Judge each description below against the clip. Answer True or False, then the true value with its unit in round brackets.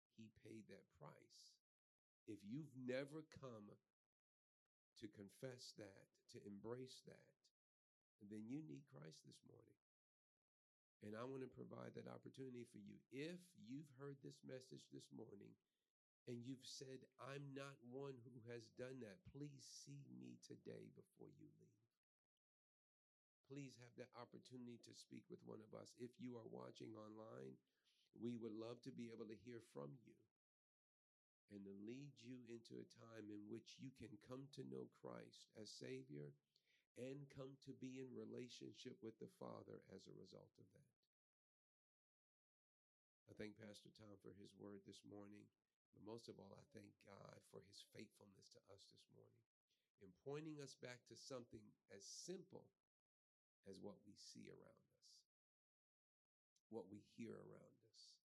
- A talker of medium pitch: False (115 Hz)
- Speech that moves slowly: False (155 wpm)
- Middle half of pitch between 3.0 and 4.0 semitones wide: False (4.5 semitones)